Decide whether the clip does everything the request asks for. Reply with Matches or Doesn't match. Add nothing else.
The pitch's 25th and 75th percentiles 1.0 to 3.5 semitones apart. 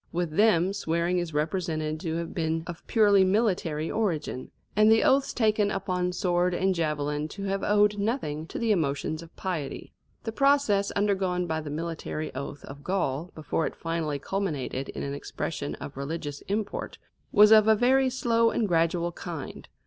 Doesn't match